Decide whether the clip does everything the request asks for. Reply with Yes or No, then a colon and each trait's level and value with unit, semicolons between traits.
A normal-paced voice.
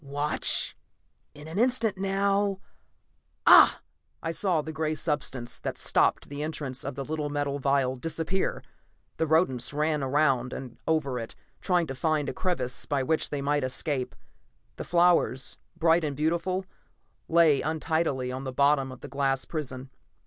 Yes: average, 155 wpm